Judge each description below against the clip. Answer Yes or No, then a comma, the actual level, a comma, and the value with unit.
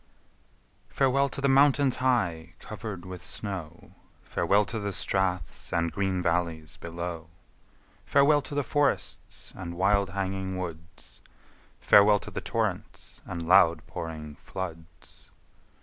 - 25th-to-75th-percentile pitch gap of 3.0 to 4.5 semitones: Yes, average, 4.2 semitones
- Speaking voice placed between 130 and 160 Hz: No, very low, 95 Hz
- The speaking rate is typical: No, slow, 120 wpm